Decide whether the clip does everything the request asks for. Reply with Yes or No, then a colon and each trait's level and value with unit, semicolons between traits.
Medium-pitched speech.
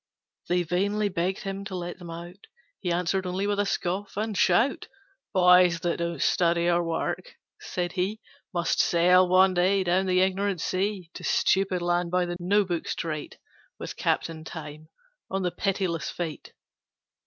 Yes: medium, 180 Hz